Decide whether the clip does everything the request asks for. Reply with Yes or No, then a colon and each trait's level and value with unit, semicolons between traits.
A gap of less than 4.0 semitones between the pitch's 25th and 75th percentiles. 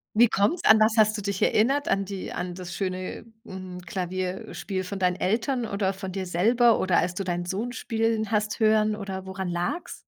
Yes: average, 2.9 semitones